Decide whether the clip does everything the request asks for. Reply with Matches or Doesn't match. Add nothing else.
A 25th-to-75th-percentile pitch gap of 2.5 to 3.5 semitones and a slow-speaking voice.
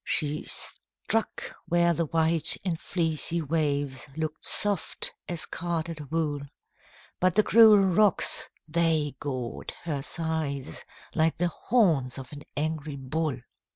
Matches